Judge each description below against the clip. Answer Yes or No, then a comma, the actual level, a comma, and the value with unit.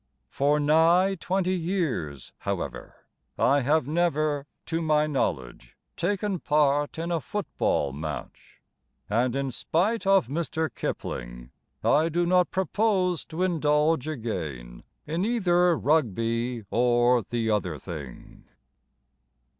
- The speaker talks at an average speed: No, slow, 115 wpm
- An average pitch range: No, wide, 6.8 semitones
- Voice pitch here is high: No, medium, 150 Hz